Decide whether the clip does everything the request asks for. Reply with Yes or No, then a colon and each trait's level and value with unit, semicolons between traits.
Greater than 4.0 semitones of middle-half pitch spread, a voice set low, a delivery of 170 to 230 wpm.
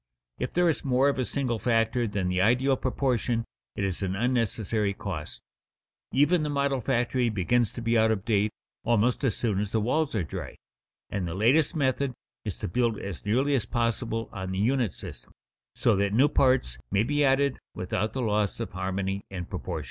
Yes: average, 4.7 semitones; low, 115 Hz; average, 195 wpm